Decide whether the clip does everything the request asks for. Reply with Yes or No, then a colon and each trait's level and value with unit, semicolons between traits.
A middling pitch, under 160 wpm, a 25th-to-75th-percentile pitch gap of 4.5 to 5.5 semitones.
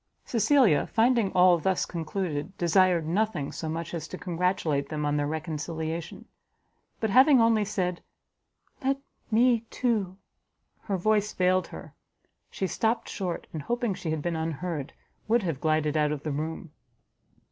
Yes: medium, 180 Hz; average, 150 wpm; average, 5.2 semitones